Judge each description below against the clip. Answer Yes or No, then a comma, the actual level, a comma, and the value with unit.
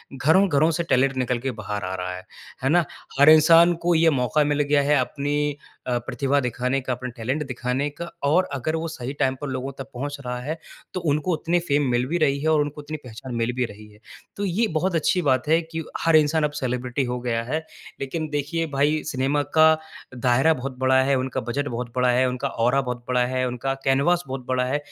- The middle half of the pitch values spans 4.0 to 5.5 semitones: No, average, 3.5 semitones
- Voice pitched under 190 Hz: Yes, medium, 140 Hz